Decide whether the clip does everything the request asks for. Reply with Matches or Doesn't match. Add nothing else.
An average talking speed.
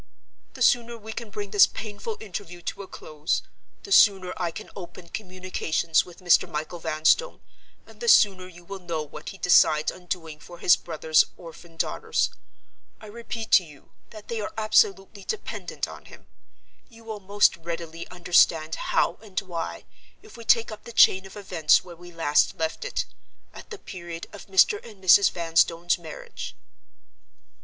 Matches